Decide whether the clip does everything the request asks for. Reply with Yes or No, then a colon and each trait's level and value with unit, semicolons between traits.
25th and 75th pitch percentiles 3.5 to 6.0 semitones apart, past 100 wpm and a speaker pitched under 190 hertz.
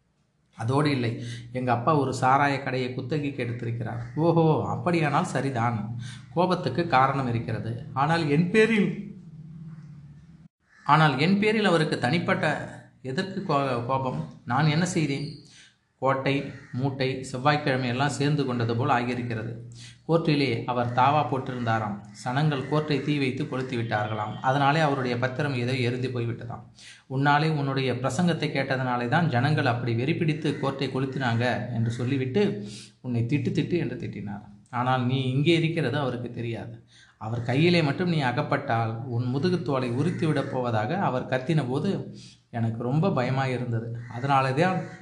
Yes: average, 4.0 semitones; average, 125 wpm; low, 135 Hz